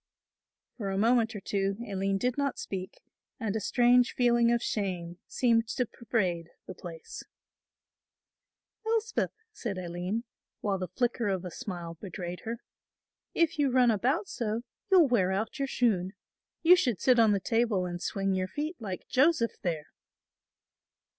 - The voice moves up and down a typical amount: Yes, average, 4.7 semitones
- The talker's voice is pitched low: No, high, 220 Hz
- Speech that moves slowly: No, average, 155 wpm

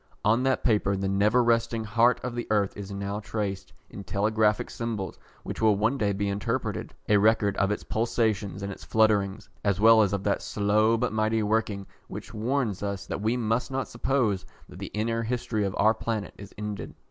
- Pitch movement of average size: No, narrow, 2.3 semitones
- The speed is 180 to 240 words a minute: Yes, average, 195 wpm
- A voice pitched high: No, low, 105 Hz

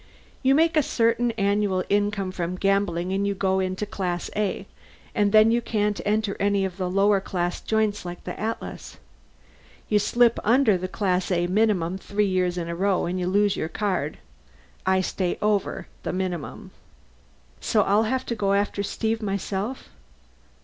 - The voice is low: No, high, 200 Hz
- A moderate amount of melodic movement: No, narrow, 2.3 semitones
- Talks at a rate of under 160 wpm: No, average, 170 wpm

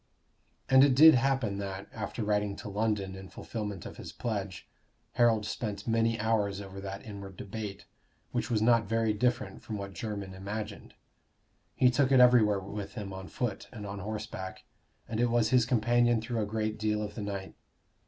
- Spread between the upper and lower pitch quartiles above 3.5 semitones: No, narrow, 2.6 semitones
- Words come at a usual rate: Yes, average, 180 wpm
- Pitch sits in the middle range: No, low, 105 Hz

